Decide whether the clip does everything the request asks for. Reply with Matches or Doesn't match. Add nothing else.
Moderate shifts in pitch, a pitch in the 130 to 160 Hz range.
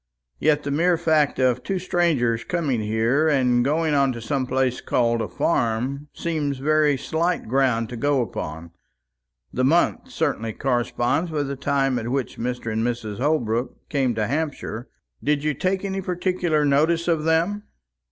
Matches